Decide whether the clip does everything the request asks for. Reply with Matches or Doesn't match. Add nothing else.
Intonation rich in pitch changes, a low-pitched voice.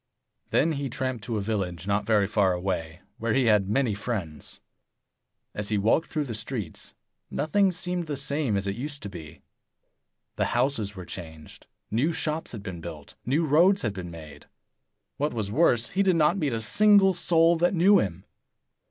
Matches